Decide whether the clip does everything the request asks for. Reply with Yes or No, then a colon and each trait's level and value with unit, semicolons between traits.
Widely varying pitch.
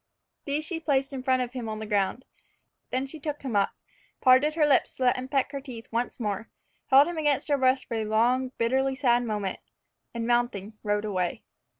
No: average, 3.4 semitones